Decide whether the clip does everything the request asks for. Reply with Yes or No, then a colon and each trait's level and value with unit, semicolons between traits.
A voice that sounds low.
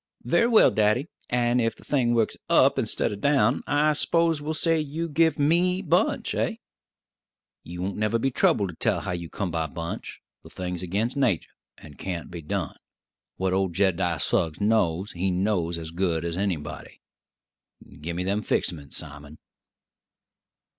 Yes: low, 100 Hz